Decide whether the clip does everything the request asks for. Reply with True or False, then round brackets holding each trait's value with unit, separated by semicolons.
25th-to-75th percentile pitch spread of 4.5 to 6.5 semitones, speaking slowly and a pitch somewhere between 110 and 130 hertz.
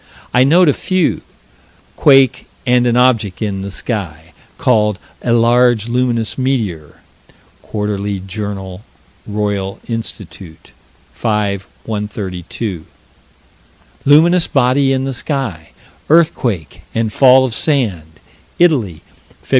True (4.8 semitones; 105 wpm; 115 Hz)